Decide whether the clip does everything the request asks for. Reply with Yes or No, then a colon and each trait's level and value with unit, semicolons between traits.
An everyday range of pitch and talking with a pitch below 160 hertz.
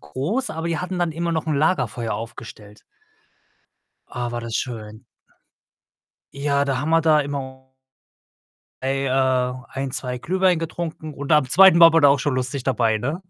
Yes: average, 4.4 semitones; medium, 140 Hz